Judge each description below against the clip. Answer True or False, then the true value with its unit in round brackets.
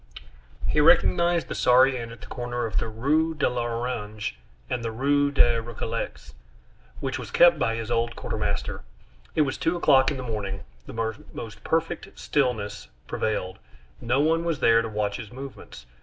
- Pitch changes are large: False (4.1 semitones)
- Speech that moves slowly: False (170 wpm)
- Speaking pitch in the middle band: False (120 Hz)